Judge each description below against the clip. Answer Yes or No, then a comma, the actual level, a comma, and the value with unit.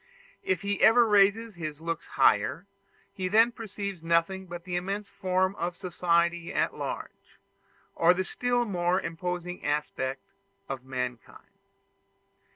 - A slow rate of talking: Yes, slow, 130 wpm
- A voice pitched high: No, medium, 180 Hz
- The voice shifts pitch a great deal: No, average, 3.1 semitones